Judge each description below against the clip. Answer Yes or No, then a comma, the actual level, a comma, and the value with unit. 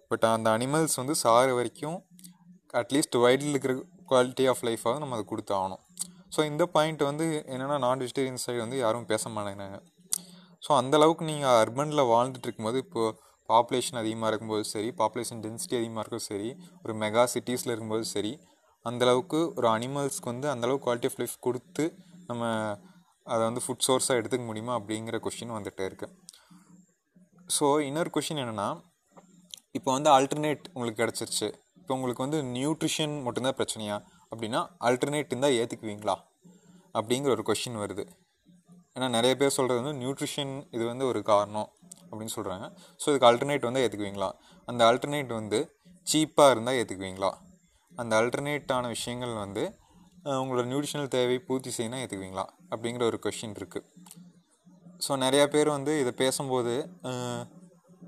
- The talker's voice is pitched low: Yes, low, 130 Hz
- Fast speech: Yes, fast, 140 wpm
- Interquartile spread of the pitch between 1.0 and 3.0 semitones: No, average, 5.0 semitones